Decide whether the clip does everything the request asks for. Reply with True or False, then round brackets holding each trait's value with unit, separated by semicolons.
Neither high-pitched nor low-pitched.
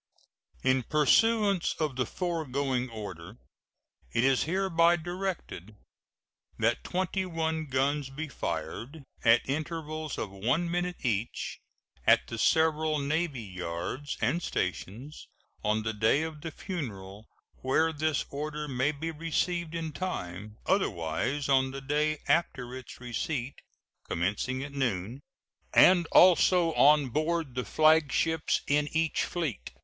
True (145 Hz)